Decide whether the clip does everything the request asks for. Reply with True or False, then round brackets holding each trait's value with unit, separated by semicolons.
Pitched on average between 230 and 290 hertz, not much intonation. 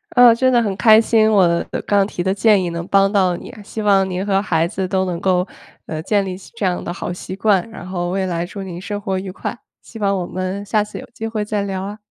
False (195 Hz; 2.3 semitones)